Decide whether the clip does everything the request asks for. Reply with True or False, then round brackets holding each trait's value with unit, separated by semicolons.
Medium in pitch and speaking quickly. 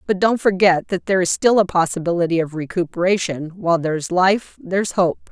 False (180 Hz; 180 wpm)